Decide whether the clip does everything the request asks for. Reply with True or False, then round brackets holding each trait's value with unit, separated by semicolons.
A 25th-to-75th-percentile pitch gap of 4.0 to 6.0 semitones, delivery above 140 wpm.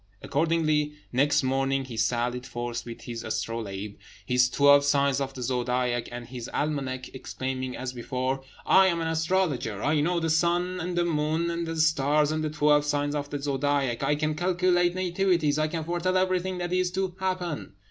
True (4.7 semitones; 180 wpm)